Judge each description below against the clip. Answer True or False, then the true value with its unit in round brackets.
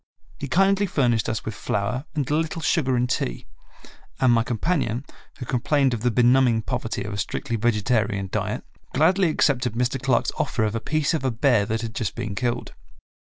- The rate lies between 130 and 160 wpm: False (195 wpm)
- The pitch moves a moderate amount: True (3.9 semitones)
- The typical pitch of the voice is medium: False (125 Hz)